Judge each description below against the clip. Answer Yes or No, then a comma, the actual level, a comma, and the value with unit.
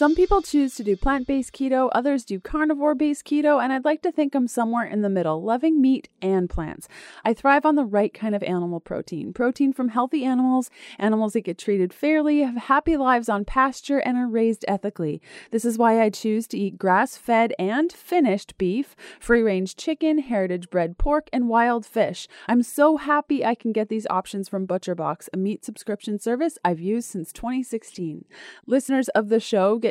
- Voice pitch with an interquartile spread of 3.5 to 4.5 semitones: No, average, 5.3 semitones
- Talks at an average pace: Yes, average, 195 wpm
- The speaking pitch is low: No, high, 235 Hz